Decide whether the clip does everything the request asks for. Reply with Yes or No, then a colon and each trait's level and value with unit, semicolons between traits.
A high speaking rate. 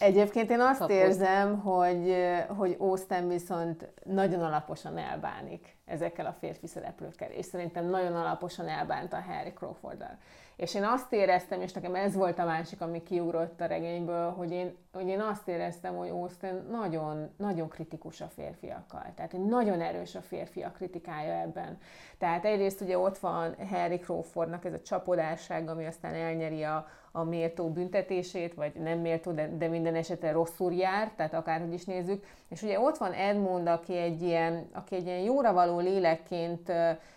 Yes: fast, 165 wpm